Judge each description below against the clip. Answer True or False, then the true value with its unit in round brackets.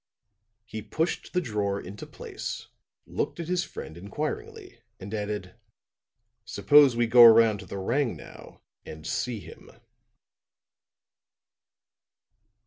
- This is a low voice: True (110 Hz)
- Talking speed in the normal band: False (110 wpm)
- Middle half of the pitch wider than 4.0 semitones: True (5.1 semitones)